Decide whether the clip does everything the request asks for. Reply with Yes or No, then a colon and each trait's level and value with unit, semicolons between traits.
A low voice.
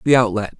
Yes: low, 115 Hz